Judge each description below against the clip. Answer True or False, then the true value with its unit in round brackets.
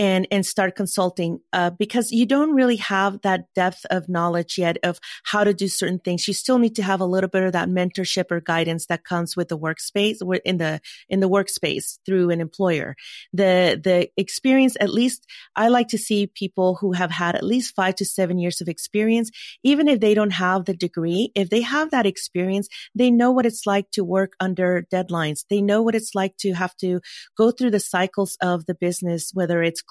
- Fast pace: True (215 wpm)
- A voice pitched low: False (190 Hz)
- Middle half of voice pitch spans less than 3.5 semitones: True (2.8 semitones)